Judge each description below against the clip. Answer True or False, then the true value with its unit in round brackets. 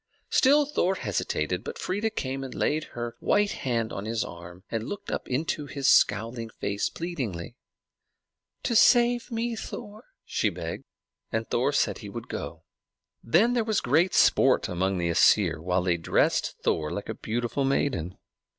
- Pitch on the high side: False (125 Hz)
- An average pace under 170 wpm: True (160 wpm)